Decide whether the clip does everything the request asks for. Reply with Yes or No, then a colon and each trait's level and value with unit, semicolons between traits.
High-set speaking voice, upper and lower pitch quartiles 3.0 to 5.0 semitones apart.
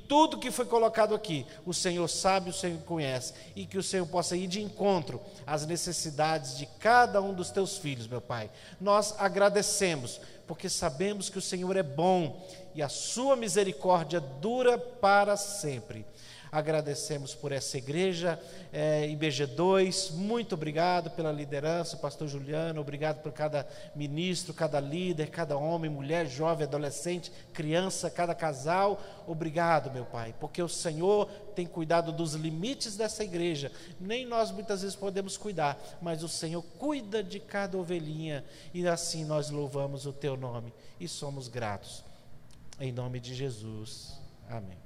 No: medium, 170 Hz; average, 4.6 semitones